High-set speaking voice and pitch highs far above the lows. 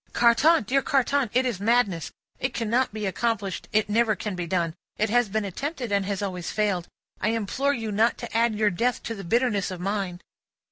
No: high, 215 Hz; average, 3.3 semitones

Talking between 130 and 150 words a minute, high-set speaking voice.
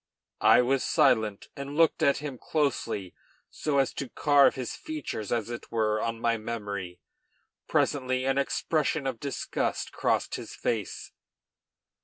No: average, 140 wpm; low, 130 Hz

